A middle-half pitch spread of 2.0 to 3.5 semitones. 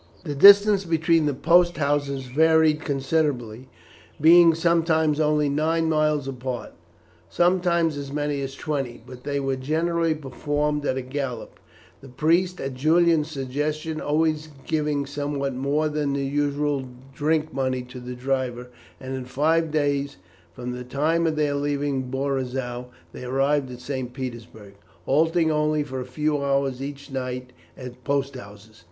Yes: average, 3.0 semitones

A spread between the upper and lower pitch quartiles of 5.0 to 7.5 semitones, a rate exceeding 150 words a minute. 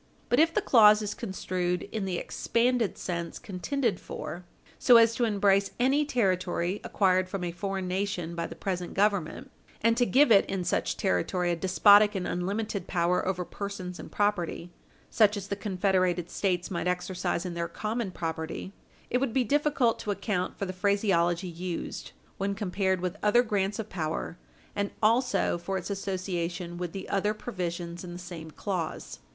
No: average, 2.9 semitones; average, 170 wpm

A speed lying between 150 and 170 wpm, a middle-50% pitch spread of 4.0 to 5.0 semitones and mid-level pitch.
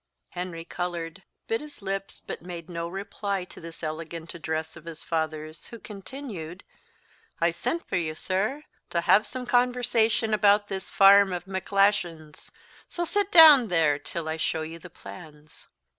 Yes: average, 160 wpm; average, 4.3 semitones; medium, 180 Hz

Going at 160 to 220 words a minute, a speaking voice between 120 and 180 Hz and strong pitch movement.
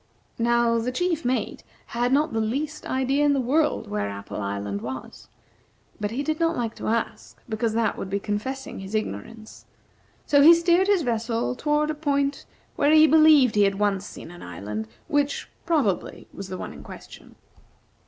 No: average, 180 wpm; high, 240 Hz; wide, 6.1 semitones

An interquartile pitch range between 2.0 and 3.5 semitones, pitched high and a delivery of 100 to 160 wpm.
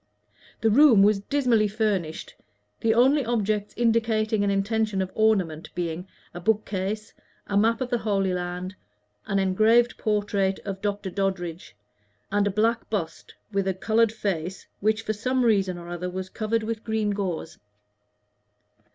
Yes: average, 2.7 semitones; high, 205 Hz; average, 150 wpm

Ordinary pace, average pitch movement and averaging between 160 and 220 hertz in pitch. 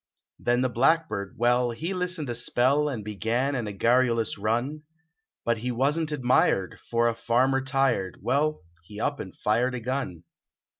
No: average, 160 wpm; average, 3.4 semitones; low, 125 Hz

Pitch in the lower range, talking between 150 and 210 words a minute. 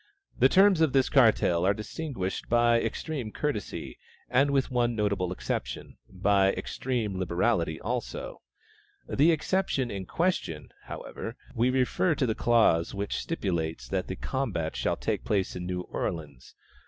No: low, 110 Hz; average, 140 wpm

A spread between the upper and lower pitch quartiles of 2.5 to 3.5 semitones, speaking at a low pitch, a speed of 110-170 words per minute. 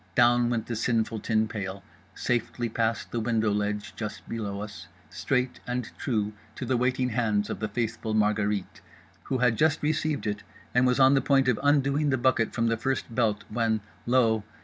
No: average, 2.8 semitones; low, 115 Hz; average, 180 wpm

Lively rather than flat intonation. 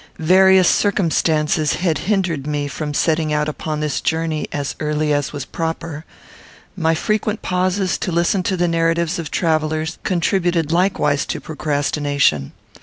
No: average, 2.8 semitones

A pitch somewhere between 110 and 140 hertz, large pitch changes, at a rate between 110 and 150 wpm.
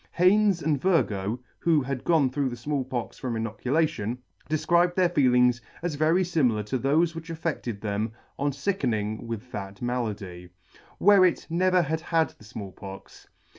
No: low, 135 Hz; wide, 6.8 semitones; average, 160 wpm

